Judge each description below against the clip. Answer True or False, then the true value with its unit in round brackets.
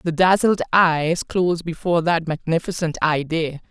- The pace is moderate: False (130 wpm)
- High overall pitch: False (165 Hz)